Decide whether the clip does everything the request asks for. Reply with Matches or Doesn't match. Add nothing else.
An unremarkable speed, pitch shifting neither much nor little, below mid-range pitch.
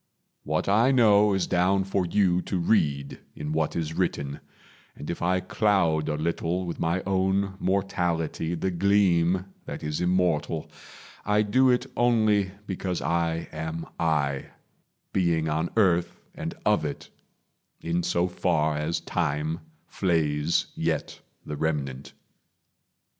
Doesn't match